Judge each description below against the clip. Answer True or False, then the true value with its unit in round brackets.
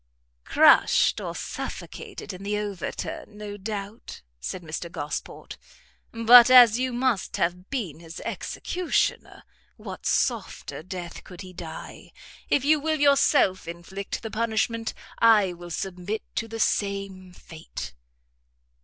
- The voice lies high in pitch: True (200 Hz)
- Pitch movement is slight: False (4.3 semitones)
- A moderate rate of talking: False (125 wpm)